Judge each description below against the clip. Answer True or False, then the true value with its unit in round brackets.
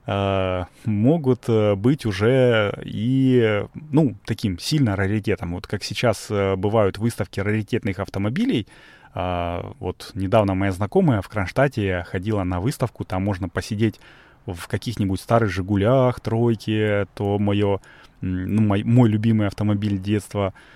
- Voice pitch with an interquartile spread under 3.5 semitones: True (2.9 semitones)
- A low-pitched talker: True (105 Hz)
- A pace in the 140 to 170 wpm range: False (115 wpm)